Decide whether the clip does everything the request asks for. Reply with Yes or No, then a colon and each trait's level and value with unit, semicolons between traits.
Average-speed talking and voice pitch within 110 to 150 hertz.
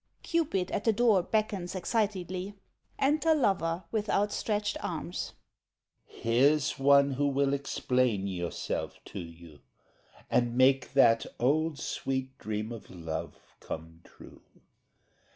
No: slow, 115 wpm; medium, 140 Hz